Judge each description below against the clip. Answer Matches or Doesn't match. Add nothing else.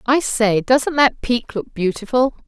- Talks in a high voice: Matches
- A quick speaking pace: Doesn't match